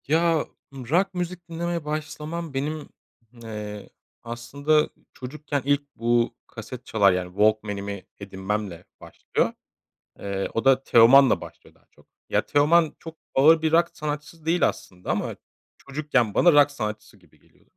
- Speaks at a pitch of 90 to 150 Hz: Yes, medium, 140 Hz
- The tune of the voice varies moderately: No, wide, 6.3 semitones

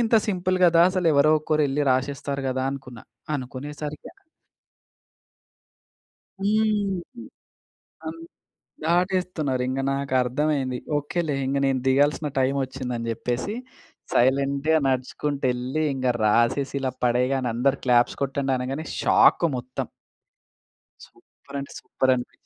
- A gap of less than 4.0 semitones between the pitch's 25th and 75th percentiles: Yes, average, 3.2 semitones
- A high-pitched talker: No, medium, 140 Hz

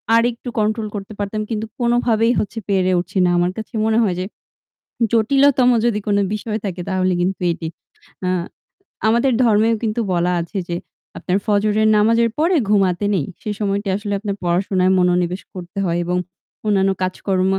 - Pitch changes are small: No, average, 3.3 semitones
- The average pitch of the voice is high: Yes, high, 205 Hz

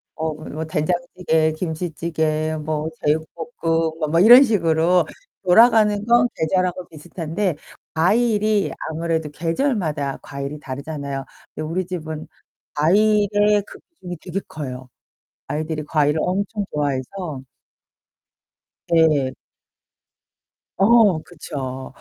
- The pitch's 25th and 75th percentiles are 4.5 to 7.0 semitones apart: No, average, 3.8 semitones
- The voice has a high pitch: No, medium, 165 Hz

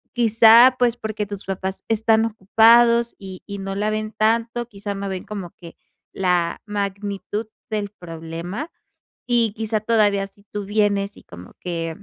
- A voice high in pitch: Yes, high, 205 Hz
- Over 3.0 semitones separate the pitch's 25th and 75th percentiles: No, narrow, 2.5 semitones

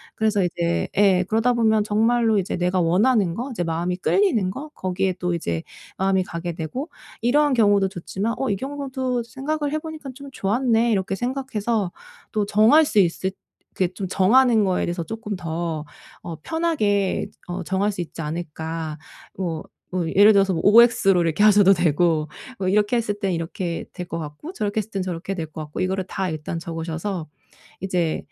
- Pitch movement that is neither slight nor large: Yes, average, 4.7 semitones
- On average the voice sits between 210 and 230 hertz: No, high, 195 Hz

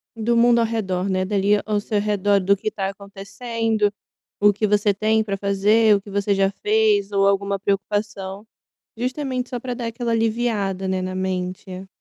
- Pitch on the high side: Yes, high, 205 Hz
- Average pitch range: No, narrow, 2.2 semitones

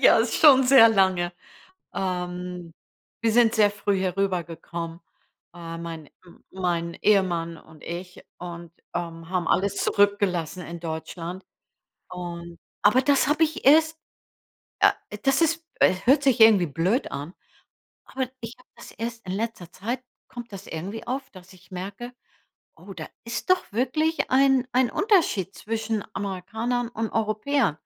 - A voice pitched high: Yes, high, 200 Hz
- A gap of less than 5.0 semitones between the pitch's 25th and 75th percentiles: No, wide, 5.6 semitones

